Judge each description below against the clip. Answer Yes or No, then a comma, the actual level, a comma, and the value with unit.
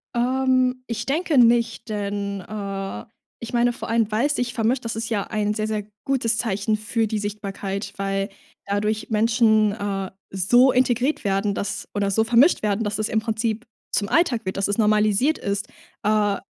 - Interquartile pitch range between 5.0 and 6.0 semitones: No, average, 2.7 semitones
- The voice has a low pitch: No, high, 215 Hz